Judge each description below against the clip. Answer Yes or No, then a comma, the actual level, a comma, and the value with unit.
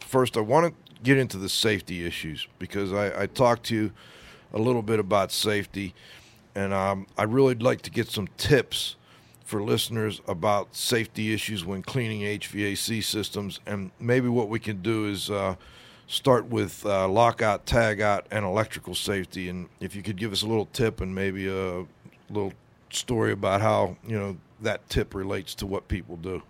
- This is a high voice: No, low, 105 Hz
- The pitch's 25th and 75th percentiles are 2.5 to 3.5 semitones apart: Yes, average, 2.8 semitones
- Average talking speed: Yes, average, 180 wpm